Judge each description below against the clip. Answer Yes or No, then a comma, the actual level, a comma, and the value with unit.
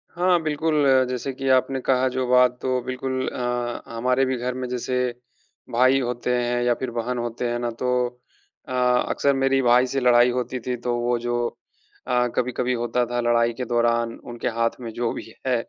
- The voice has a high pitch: No, low, 125 Hz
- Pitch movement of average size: No, narrow, 1.3 semitones